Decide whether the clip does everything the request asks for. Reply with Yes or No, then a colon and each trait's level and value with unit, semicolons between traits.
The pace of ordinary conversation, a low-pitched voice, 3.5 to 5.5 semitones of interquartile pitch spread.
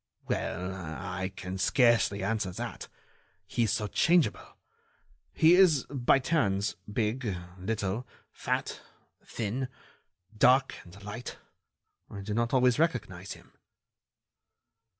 No: slow, 110 wpm; low, 110 Hz; average, 4.7 semitones